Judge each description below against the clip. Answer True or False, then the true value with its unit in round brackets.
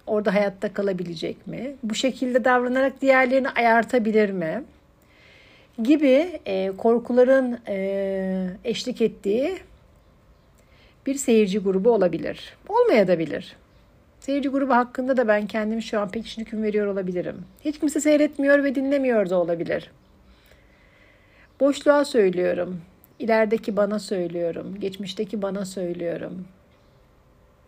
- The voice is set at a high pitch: True (220 Hz)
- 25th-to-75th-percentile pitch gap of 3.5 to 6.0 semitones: True (5.3 semitones)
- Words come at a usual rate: True (110 wpm)